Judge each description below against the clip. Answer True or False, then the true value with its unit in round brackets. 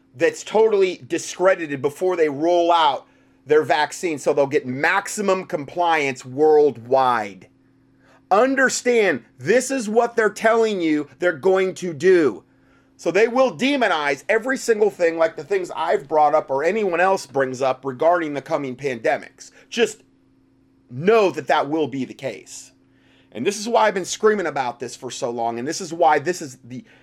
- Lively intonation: True (7.3 semitones)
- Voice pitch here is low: False (170 Hz)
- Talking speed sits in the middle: True (165 wpm)